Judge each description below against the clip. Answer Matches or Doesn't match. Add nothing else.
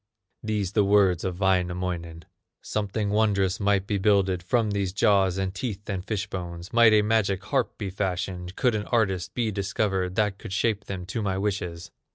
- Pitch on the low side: Matches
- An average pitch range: Doesn't match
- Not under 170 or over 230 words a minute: Matches